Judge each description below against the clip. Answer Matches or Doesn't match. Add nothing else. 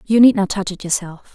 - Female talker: Matches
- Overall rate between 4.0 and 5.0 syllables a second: Doesn't match